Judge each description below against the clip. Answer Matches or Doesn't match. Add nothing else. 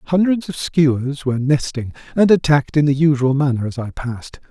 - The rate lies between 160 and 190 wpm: Matches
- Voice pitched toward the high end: Doesn't match